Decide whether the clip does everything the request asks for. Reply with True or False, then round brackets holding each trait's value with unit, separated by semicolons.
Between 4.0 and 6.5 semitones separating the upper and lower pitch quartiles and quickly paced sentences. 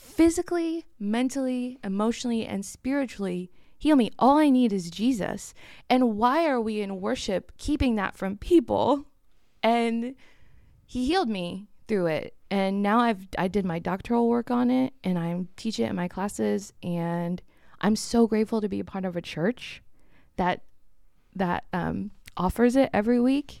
False (4.8 semitones; 160 wpm)